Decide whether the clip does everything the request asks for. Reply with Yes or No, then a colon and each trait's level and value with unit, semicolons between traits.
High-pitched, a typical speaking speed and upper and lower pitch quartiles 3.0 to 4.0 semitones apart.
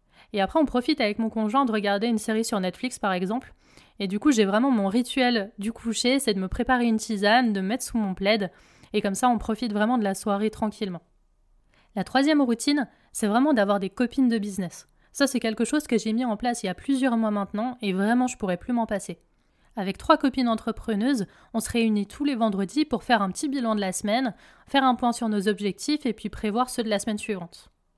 No: high, 225 Hz; fast, 235 wpm; average, 3.5 semitones